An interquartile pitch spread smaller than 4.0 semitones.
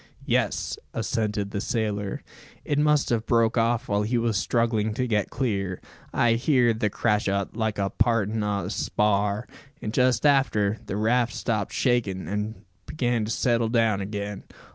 Yes: narrow, 2.5 semitones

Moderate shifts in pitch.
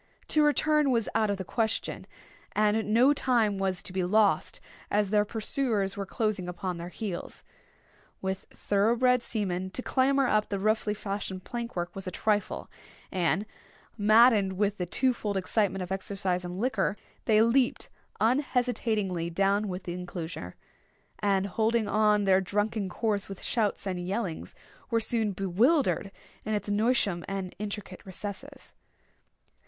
Yes: average, 3.0 semitones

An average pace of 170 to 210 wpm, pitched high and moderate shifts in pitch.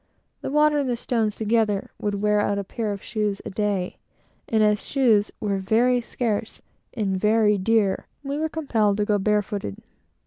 No: average, 175 wpm; high, 210 Hz; narrow, 2.3 semitones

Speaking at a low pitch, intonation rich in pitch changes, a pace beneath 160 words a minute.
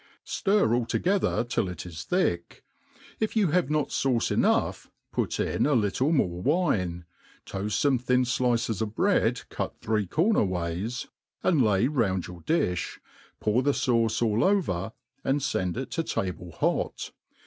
Yes: low, 115 Hz; wide, 7.4 semitones; average, 150 wpm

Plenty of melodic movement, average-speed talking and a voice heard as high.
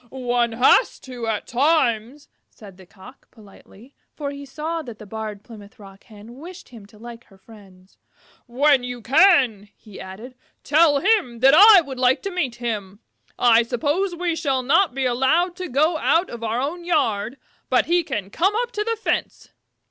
Yes: wide, 6.3 semitones; average, 180 wpm; very high, 255 Hz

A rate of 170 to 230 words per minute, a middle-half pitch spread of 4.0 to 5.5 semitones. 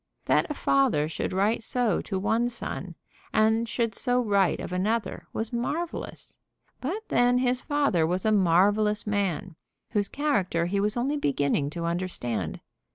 No: average, 155 wpm; average, 5.1 semitones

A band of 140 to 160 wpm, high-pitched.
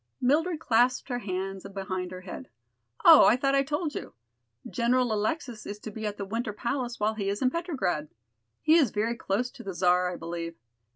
No: average, 195 wpm; high, 220 Hz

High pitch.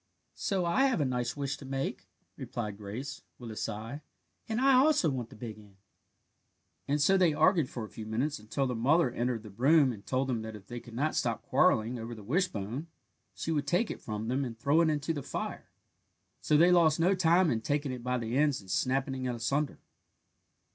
No: low, 130 Hz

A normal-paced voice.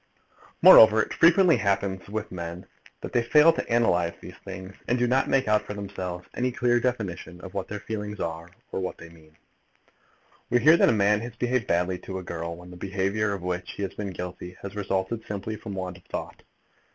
No: fast, 210 wpm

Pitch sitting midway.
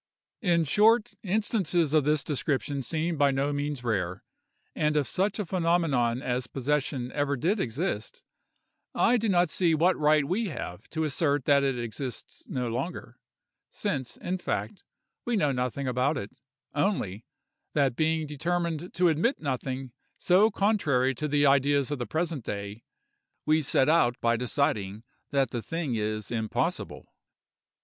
Yes: medium, 145 Hz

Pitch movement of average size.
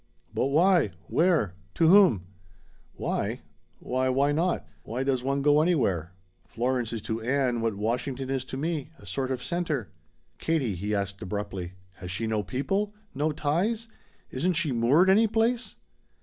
No: wide, 6.6 semitones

